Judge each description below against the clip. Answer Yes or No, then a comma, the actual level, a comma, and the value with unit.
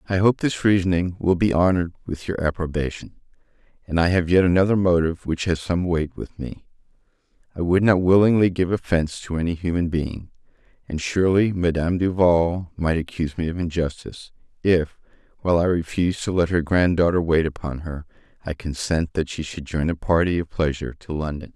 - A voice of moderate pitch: No, very low, 85 Hz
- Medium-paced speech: Yes, average, 180 wpm